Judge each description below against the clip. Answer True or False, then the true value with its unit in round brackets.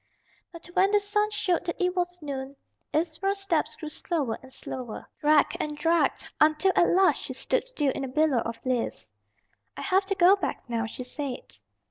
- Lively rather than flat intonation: True (5.9 semitones)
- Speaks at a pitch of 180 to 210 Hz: False (320 Hz)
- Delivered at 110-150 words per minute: False (185 wpm)